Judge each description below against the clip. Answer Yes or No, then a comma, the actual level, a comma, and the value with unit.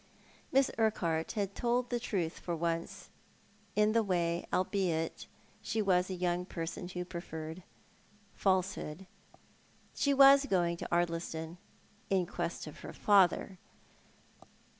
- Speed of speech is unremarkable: No, slow, 125 wpm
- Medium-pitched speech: Yes, medium, 180 Hz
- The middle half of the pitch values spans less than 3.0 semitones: No, average, 3.4 semitones